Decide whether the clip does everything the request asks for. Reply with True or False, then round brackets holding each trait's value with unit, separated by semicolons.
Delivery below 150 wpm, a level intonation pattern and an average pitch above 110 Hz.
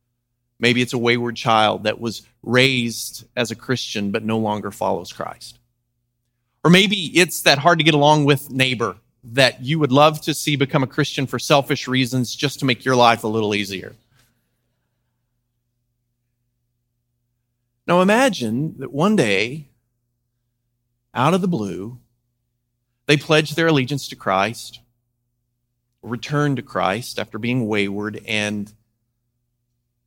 True (135 wpm; 2.0 semitones; 120 Hz)